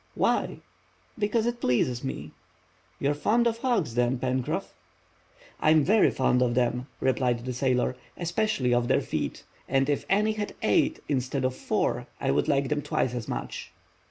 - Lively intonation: Yes, wide, 7.6 semitones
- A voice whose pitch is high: No, low, 135 Hz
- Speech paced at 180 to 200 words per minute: No, average, 170 wpm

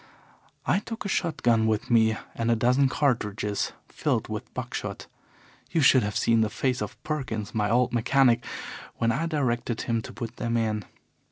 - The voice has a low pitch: Yes, low, 120 Hz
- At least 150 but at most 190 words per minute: Yes, average, 180 wpm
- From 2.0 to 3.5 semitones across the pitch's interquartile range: Yes, average, 3.0 semitones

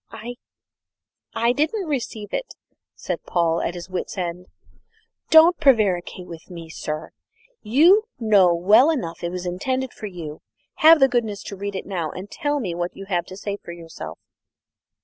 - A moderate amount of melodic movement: No, wide, 6.7 semitones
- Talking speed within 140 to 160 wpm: No, average, 170 wpm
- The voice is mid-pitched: No, high, 200 Hz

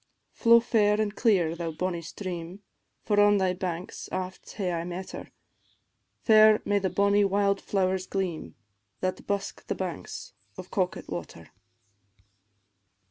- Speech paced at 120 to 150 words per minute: Yes, slow, 135 wpm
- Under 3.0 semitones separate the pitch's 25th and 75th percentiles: Yes, narrow, 2.5 semitones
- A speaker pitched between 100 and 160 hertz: No, high, 190 Hz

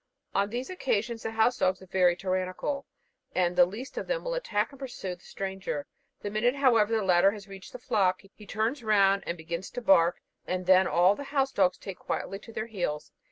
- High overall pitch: Yes, high, 200 Hz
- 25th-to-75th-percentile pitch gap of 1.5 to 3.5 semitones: No, average, 4.2 semitones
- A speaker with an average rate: No, fast, 215 wpm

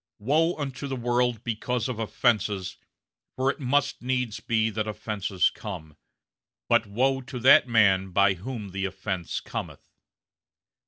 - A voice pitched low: Yes, low, 115 Hz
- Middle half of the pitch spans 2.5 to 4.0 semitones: No, average, 4.5 semitones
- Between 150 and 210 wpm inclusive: No, average, 140 wpm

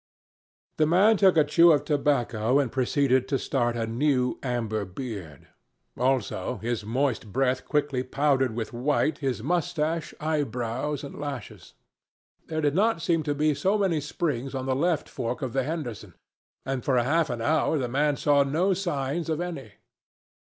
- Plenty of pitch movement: No, average, 3.8 semitones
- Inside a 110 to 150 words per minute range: No, average, 165 wpm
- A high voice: No, medium, 140 Hz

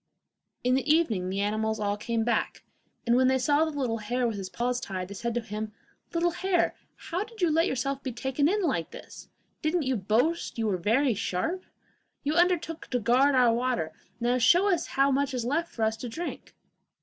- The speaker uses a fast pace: Yes, fast, 210 wpm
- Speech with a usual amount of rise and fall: No, wide, 5.8 semitones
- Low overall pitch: No, very high, 250 Hz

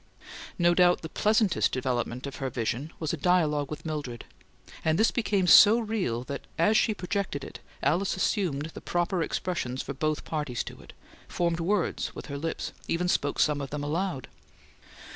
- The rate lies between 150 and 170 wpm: No, average, 180 wpm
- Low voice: No, medium, 160 Hz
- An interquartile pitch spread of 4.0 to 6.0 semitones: Yes, average, 4.5 semitones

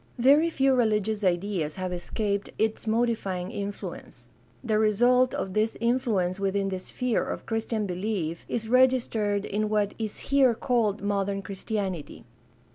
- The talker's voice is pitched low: No, high, 210 Hz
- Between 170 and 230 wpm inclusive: No, slow, 135 wpm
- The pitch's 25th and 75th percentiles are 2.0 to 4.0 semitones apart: Yes, average, 3.0 semitones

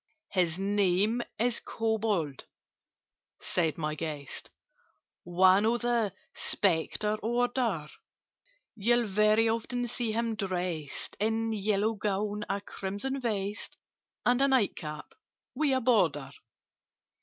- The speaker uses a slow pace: Yes, slow, 110 wpm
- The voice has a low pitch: No, high, 210 Hz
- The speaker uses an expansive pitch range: No, average, 3.8 semitones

